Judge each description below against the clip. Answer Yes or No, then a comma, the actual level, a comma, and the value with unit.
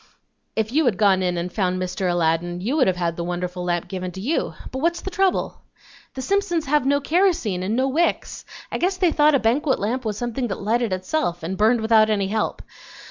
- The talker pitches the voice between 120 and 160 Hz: No, high, 220 Hz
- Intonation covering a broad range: Yes, wide, 7.8 semitones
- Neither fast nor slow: No, fast, 220 wpm